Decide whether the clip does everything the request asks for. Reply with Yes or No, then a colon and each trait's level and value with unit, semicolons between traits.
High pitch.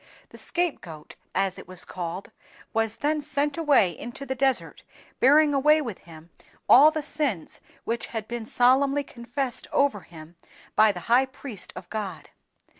Yes: high, 240 Hz